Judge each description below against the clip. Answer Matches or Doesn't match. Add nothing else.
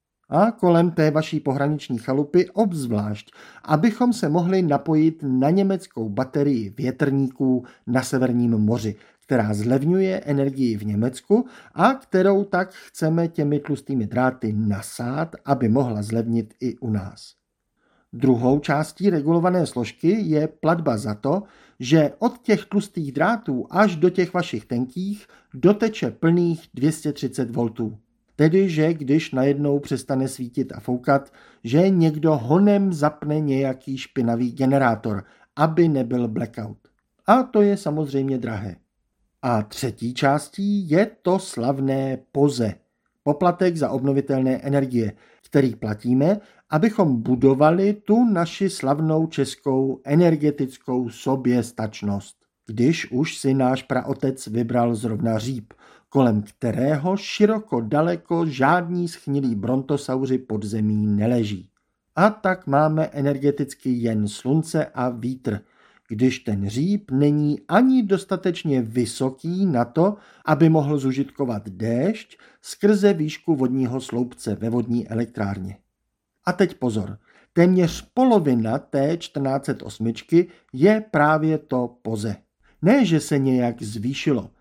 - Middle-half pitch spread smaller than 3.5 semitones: Doesn't match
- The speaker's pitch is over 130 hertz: Matches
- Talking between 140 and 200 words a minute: Doesn't match